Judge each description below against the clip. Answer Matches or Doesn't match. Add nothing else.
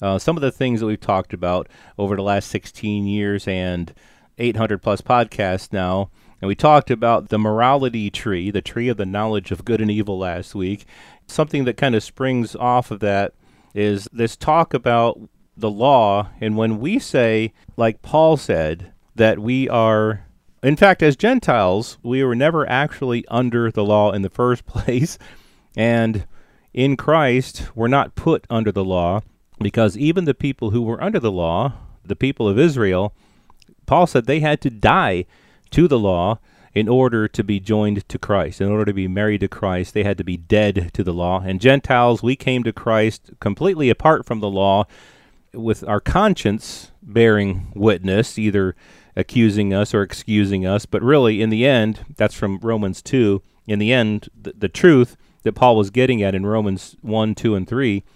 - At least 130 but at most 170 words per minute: Doesn't match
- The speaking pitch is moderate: Doesn't match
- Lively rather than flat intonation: Doesn't match